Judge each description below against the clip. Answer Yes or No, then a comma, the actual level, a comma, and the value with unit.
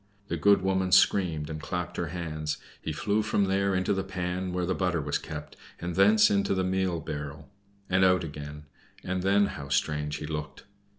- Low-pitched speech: Yes, very low, 90 Hz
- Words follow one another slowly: No, average, 190 wpm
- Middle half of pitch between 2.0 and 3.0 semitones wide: No, average, 3.8 semitones